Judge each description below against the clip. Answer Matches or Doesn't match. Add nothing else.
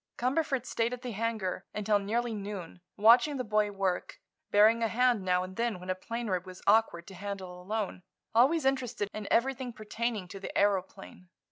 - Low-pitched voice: Doesn't match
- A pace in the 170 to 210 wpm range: Matches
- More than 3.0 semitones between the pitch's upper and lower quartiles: Matches